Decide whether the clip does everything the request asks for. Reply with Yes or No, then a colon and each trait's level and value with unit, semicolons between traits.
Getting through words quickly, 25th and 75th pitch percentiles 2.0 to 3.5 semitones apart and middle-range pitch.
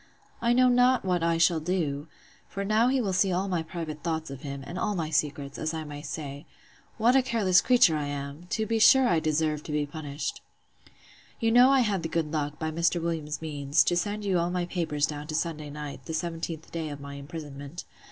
No: fast, 220 wpm; average, 4.1 semitones; medium, 165 Hz